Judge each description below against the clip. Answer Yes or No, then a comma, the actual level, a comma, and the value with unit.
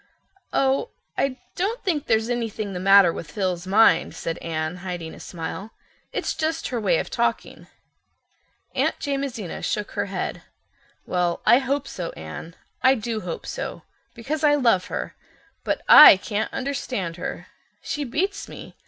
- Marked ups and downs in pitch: Yes, wide, 7.3 semitones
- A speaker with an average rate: Yes, average, 150 wpm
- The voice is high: Yes, high, 220 Hz